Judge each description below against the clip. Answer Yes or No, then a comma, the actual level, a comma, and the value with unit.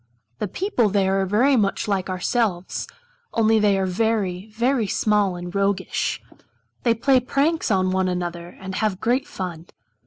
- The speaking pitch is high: Yes, high, 200 Hz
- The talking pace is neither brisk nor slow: Yes, average, 150 wpm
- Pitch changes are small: No, average, 3.5 semitones